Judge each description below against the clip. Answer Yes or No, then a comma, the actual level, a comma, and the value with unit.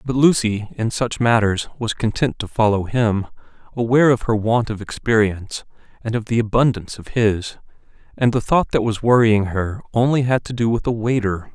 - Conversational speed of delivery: Yes, average, 185 wpm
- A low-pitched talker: Yes, low, 115 Hz